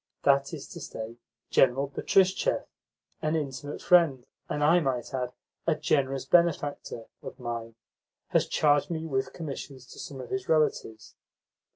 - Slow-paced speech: No, average, 145 wpm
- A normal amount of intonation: Yes, average, 3.6 semitones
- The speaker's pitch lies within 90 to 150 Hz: Yes, medium, 140 Hz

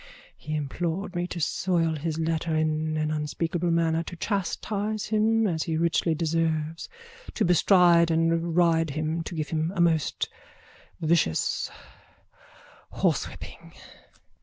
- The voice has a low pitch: No, medium, 165 Hz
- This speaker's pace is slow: Yes, slow, 125 wpm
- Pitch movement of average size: No, narrow, 1.8 semitones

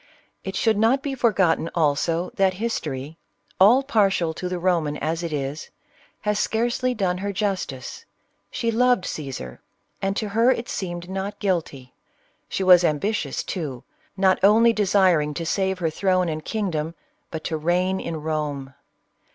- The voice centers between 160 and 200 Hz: Yes, medium, 185 Hz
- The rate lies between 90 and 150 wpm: No, average, 160 wpm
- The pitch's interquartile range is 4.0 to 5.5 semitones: Yes, average, 4.6 semitones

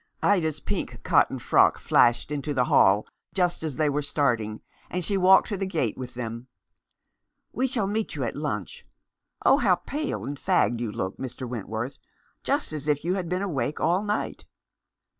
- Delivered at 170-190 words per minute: Yes, average, 180 wpm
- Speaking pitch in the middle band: Yes, medium, 150 Hz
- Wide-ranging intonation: Yes, wide, 7.4 semitones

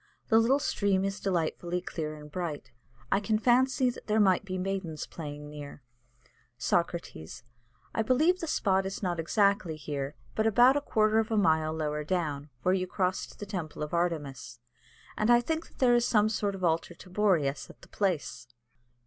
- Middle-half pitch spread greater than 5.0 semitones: Yes, wide, 5.5 semitones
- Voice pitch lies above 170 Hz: Yes, medium, 185 Hz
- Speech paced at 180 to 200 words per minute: Yes, average, 190 wpm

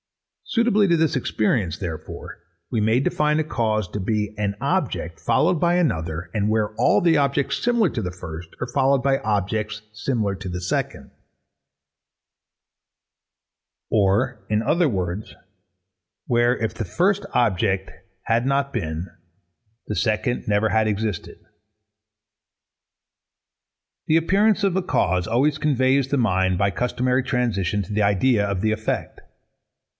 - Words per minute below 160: Yes, average, 140 wpm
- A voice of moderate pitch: No, low, 110 Hz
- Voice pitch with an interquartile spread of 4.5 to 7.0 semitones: Yes, wide, 5.5 semitones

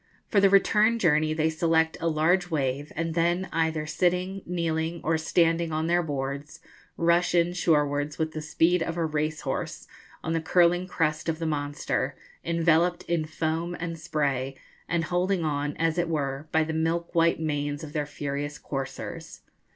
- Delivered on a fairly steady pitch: Yes, narrow, 2.1 semitones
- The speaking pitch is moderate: Yes, medium, 160 Hz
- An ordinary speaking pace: Yes, average, 165 wpm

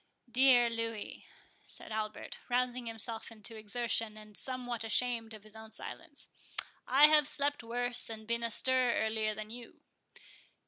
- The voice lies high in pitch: Yes, high, 230 Hz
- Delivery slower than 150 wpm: Yes, average, 140 wpm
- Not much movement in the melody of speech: Yes, narrow, 2.1 semitones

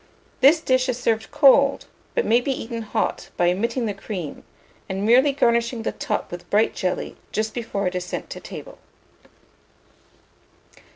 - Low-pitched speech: No, high, 230 Hz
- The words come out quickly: No, average, 160 wpm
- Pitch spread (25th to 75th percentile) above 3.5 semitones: Yes, average, 4.3 semitones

